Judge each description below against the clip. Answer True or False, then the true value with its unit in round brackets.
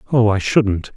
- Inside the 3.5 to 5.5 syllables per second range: True (4.4 syllables/s)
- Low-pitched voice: True (110 Hz)